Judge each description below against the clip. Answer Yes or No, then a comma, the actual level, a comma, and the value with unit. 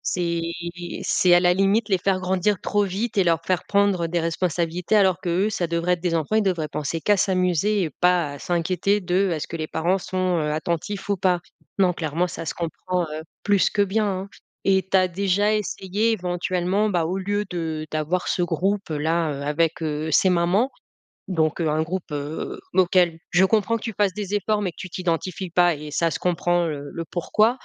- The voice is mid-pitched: Yes, medium, 180 Hz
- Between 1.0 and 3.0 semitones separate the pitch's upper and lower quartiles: Yes, average, 2.7 semitones